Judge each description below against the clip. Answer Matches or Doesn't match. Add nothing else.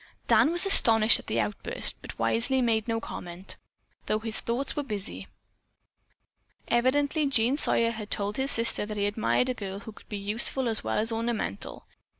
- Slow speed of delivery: Doesn't match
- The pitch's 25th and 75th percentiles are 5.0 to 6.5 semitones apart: Doesn't match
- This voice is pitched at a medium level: Doesn't match